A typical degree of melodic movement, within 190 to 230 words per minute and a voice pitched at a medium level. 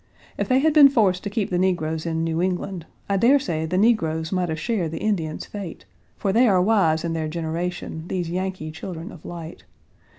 Yes: average, 3.7 semitones; fast, 205 wpm; medium, 180 Hz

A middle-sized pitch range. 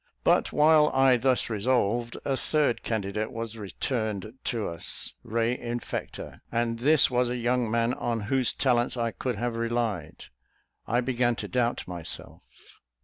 No: narrow, 2.1 semitones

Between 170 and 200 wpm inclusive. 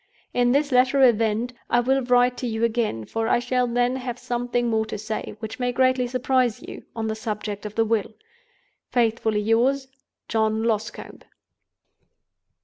No: average, 160 wpm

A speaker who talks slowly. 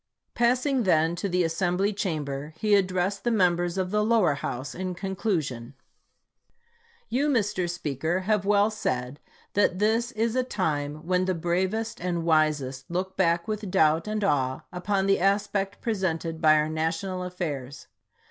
No: average, 160 wpm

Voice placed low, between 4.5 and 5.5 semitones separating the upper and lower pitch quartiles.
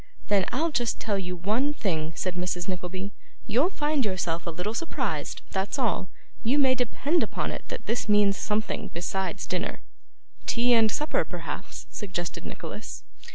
No: high, 205 Hz; average, 5.2 semitones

